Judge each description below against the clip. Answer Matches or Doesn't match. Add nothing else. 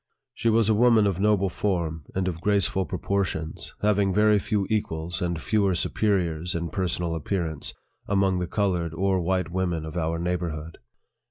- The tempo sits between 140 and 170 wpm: Matches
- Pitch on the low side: Matches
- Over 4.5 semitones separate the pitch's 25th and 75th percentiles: Doesn't match